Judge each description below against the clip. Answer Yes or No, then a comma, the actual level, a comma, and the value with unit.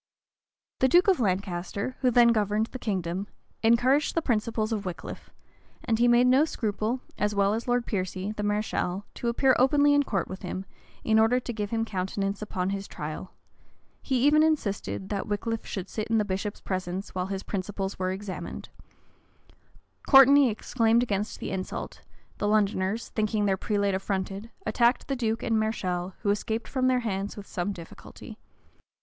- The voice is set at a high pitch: Yes, high, 210 Hz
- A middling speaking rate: Yes, average, 170 wpm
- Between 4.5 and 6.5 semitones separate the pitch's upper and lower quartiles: No, average, 3.5 semitones